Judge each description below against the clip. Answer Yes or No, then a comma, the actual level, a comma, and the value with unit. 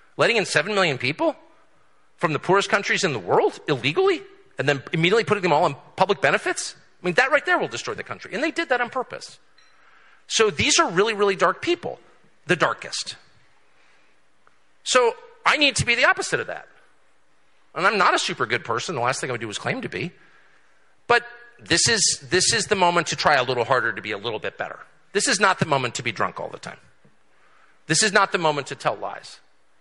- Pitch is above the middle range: Yes, high, 215 Hz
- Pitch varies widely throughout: Yes, wide, 9.0 semitones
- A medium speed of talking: No, fast, 220 wpm